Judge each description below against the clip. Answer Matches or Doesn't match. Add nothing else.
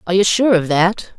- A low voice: Doesn't match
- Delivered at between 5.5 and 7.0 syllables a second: Matches